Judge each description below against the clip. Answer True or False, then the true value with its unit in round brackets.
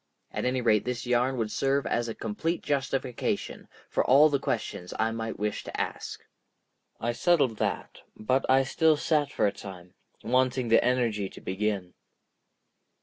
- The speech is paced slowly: False (160 wpm)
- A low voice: True (125 Hz)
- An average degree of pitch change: True (3.9 semitones)